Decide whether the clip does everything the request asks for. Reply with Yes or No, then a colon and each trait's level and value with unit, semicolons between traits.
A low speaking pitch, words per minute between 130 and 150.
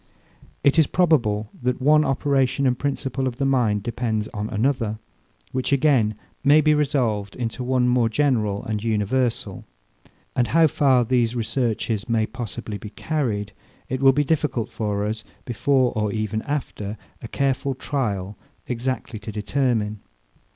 Yes: low, 125 Hz; average, 145 wpm